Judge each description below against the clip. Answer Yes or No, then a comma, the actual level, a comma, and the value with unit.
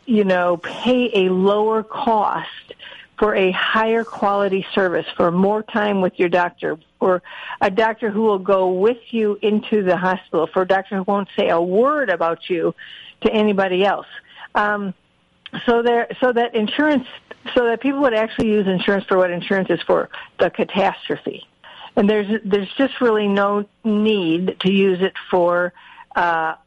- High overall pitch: Yes, high, 205 Hz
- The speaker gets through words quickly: No, average, 165 wpm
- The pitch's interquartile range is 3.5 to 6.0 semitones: No, average, 3.0 semitones